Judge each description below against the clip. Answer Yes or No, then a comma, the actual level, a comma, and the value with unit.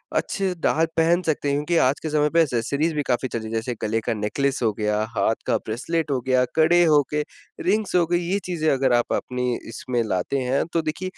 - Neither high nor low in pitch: Yes, medium, 145 Hz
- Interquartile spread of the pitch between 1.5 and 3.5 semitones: No, average, 5.3 semitones